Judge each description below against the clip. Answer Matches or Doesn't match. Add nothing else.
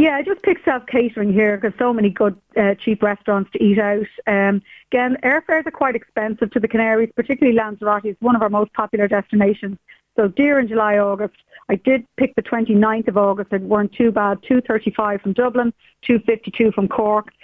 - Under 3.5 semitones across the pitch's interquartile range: Matches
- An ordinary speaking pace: Matches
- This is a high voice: Matches